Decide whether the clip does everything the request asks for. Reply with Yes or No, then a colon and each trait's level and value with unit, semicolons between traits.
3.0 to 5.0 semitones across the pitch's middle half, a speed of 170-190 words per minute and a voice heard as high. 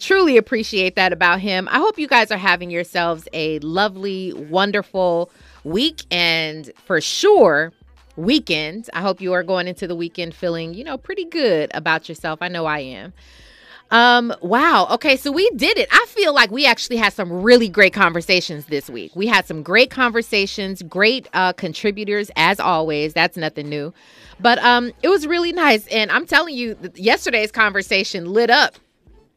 No: wide, 5.5 semitones; average, 175 wpm; high, 195 Hz